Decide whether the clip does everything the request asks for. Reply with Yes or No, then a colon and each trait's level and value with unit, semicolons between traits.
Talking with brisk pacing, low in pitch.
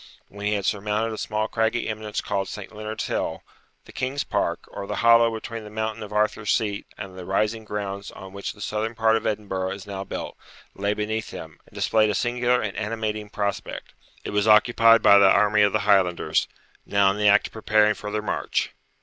Yes: fast, 210 wpm; low, 105 Hz